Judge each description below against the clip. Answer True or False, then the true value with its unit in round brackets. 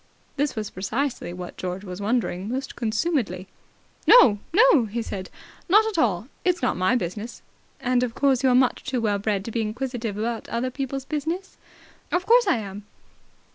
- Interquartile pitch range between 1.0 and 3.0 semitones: False (5.0 semitones)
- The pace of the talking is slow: False (175 wpm)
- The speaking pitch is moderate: False (240 Hz)